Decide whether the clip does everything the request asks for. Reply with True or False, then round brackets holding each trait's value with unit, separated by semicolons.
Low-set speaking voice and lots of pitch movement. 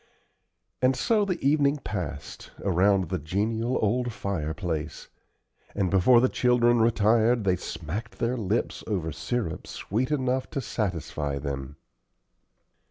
True (105 Hz; 5.8 semitones)